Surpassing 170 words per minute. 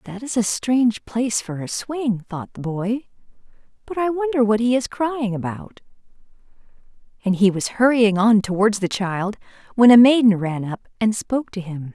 Yes: average, 180 wpm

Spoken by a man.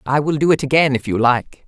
No: female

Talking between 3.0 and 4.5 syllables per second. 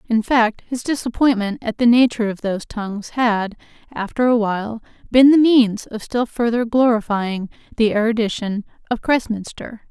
No: 5.0 syllables/s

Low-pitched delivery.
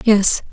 No: high, 210 Hz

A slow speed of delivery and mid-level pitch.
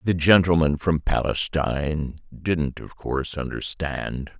No: slow, 110 wpm; very low, 80 Hz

